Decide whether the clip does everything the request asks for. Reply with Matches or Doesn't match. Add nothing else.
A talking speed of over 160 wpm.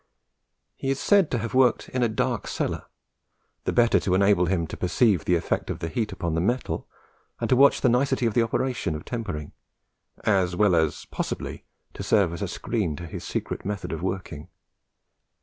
Matches